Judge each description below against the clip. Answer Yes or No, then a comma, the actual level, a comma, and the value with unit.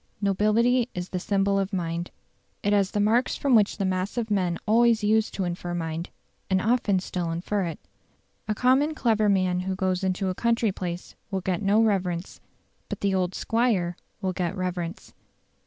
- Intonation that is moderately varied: Yes, average, 3.1 semitones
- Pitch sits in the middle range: No, high, 195 Hz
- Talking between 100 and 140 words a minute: No, average, 180 wpm